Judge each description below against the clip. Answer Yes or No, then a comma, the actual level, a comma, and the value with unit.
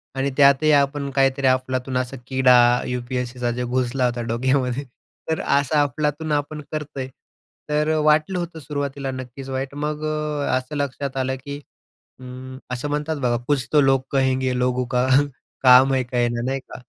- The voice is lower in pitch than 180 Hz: Yes, low, 135 Hz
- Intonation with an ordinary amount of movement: No, narrow, 2.3 semitones